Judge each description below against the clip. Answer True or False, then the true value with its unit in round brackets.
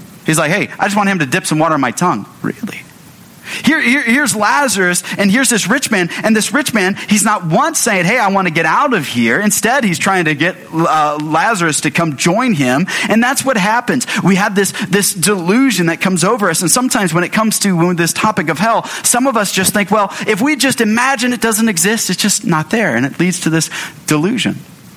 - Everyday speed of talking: False (235 wpm)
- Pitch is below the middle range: False (200 Hz)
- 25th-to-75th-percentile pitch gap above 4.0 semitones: True (4.6 semitones)